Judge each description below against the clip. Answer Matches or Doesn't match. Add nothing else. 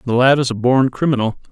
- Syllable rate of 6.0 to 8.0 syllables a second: Matches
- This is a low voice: Matches